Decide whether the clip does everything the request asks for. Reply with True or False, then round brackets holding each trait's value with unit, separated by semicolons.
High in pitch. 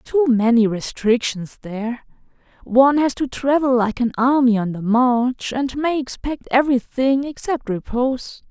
True (250 Hz)